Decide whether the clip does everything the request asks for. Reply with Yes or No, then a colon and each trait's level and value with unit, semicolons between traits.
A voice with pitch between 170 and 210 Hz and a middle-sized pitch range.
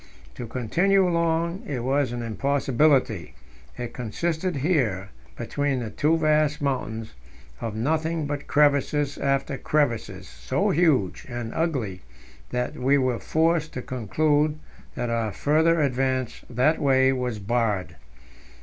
No: low, 135 Hz; average, 4.6 semitones